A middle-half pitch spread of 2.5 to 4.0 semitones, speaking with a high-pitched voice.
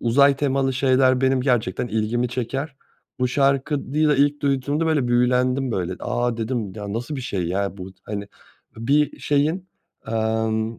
No: average, 3.7 semitones; low, 125 Hz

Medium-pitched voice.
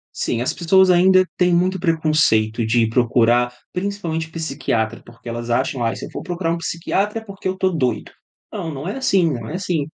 Yes: medium, 165 Hz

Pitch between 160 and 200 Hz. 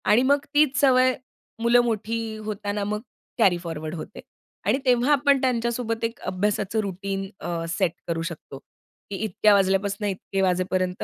No: high, 210 Hz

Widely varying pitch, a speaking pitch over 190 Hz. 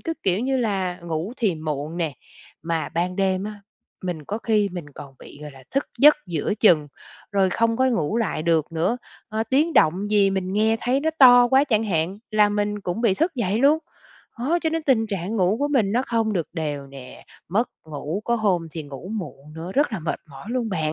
Yes: wide, 5.8 semitones; high, 200 Hz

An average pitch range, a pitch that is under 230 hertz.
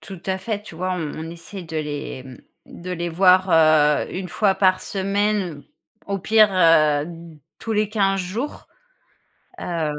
Yes: average, 3.5 semitones; medium, 185 Hz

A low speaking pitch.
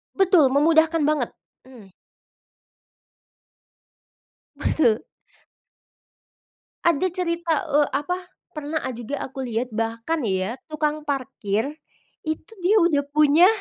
No: very high, 295 Hz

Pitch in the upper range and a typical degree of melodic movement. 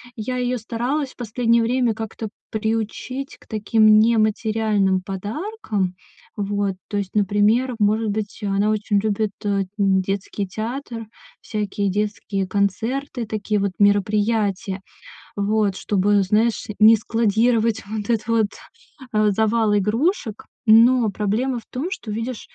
No: high, 215 Hz; narrow, 2.1 semitones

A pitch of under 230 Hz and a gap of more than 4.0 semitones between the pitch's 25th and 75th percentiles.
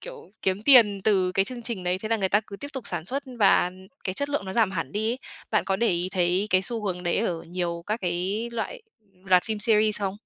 No: high, 200 Hz; average, 3.6 semitones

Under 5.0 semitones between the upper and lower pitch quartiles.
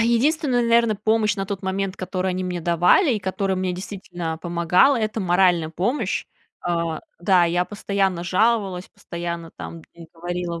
Yes: average, 3.3 semitones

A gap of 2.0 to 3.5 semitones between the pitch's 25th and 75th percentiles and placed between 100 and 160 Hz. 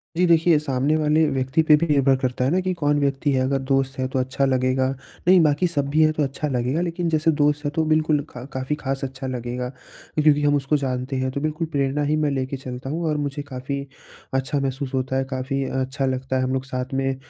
Yes: narrow, 2.5 semitones; medium, 140 Hz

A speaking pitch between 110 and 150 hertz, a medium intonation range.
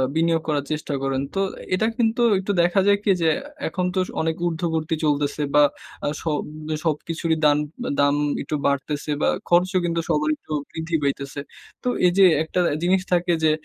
No: medium, 160 Hz; average, 3.1 semitones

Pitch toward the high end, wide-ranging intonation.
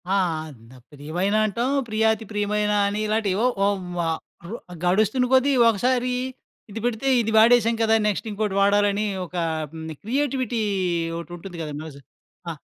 No: high, 210 Hz; average, 3.7 semitones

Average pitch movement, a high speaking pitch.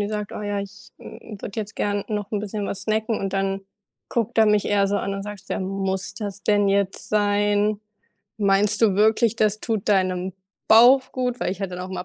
No: narrow, 1.5 semitones; high, 205 Hz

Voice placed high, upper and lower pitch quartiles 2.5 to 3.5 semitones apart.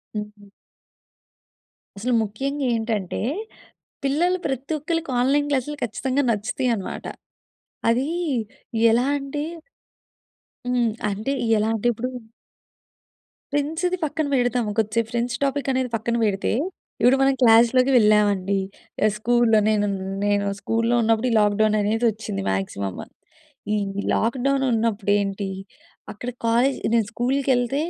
No: high, 235 Hz; average, 4.1 semitones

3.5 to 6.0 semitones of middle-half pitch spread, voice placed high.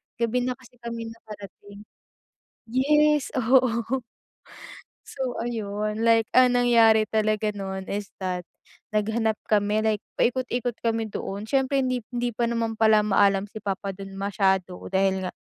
No: average, 3.1 semitones; high, 220 Hz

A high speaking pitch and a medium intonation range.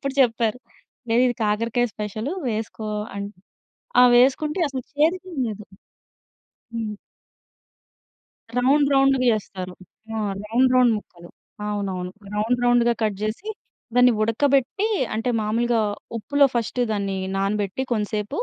Yes: high, 230 Hz; average, 3.4 semitones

